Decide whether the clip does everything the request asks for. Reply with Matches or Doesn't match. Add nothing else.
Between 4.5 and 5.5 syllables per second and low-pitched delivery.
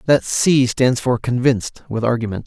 Matches